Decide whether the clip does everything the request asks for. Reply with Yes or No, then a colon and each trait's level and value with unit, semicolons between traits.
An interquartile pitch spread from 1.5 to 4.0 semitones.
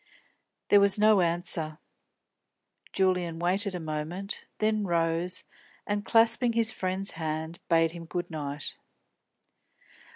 Yes: average, 3.5 semitones